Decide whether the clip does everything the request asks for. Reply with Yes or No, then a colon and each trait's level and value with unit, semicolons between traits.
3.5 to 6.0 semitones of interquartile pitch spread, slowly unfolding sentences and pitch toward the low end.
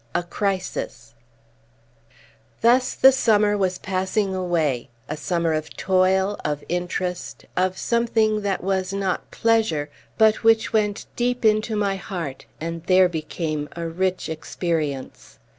No: average, 4.1 semitones; slow, 125 wpm; medium, 185 Hz